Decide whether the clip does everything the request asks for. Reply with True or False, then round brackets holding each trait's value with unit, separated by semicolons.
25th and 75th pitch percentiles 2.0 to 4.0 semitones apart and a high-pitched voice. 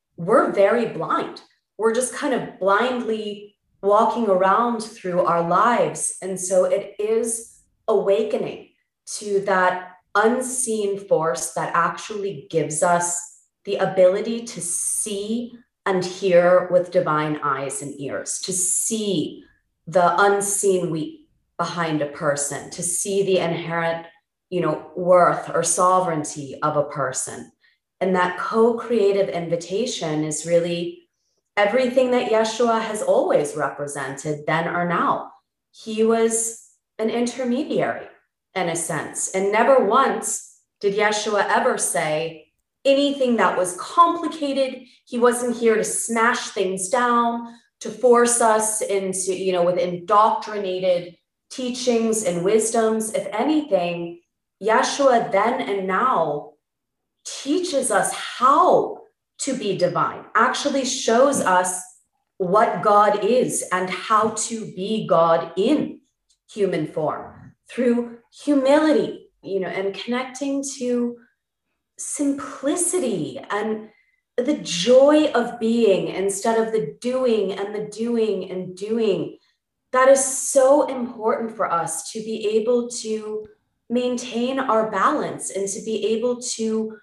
False (4.9 semitones; 210 Hz)